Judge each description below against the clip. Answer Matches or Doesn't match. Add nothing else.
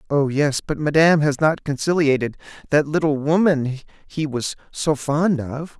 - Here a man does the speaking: Matches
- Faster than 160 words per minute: Doesn't match